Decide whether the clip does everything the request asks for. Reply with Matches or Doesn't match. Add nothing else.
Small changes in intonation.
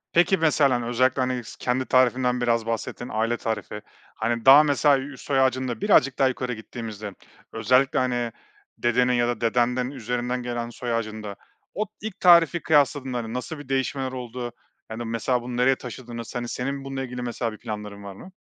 Matches